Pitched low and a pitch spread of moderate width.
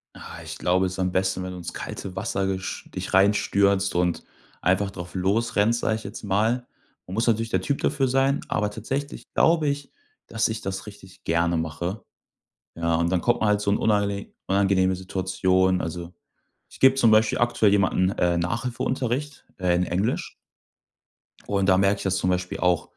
Yes: low, 100 Hz; average, 3.4 semitones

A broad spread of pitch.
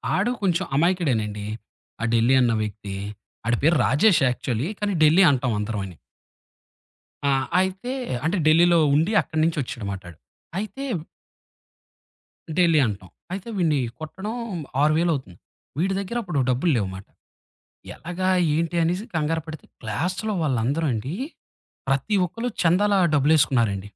Yes: wide, 7.3 semitones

